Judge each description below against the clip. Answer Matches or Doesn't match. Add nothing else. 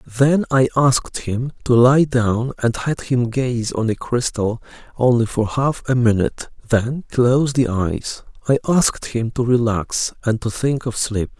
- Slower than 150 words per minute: Doesn't match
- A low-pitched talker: Matches